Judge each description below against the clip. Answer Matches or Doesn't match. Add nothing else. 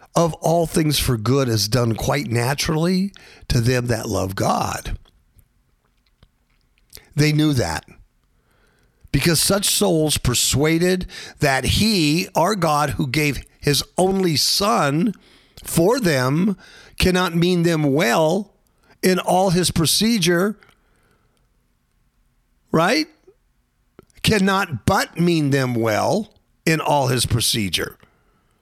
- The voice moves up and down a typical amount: Doesn't match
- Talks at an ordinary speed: Doesn't match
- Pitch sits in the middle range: Matches